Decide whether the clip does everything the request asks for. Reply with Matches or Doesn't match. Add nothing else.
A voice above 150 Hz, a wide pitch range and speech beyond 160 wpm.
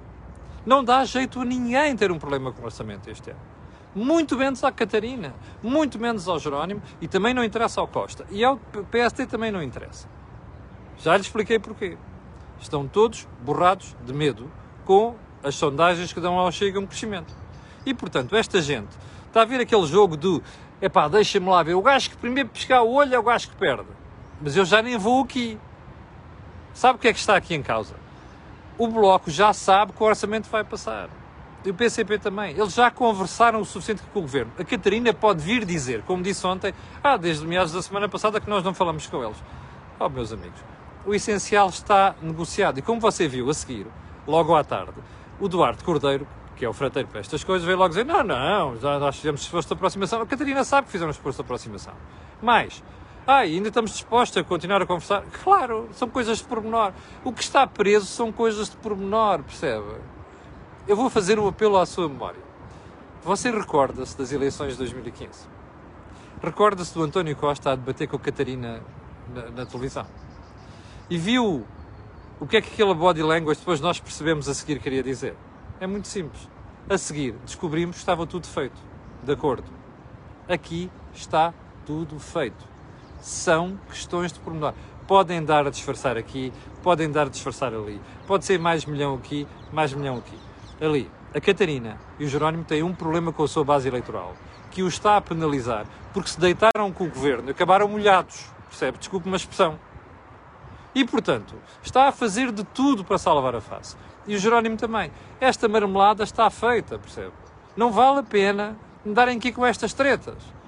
Matches